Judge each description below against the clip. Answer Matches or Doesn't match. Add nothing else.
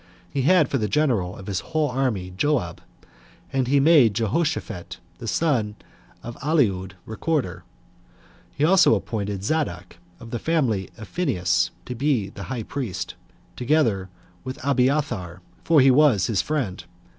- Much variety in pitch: Matches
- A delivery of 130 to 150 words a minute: Matches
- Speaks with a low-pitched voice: Matches